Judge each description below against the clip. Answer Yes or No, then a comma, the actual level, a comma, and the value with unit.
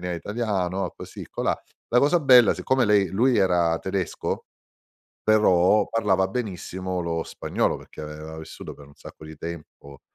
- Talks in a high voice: No, very low, 95 Hz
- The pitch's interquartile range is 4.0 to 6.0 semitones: Yes, average, 4.5 semitones